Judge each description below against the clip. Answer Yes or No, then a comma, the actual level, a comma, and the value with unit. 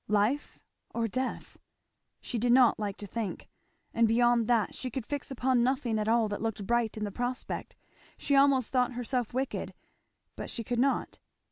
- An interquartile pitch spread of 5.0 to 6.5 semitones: No, narrow, 2.6 semitones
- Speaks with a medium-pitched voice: No, high, 240 Hz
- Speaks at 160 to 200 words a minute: Yes, average, 175 wpm